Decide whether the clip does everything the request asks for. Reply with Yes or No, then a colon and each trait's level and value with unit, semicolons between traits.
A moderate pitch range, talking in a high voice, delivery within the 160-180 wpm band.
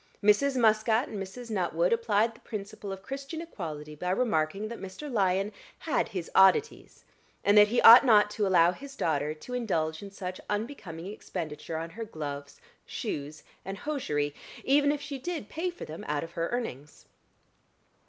No: wide, 6.3 semitones; high, 200 Hz; average, 170 wpm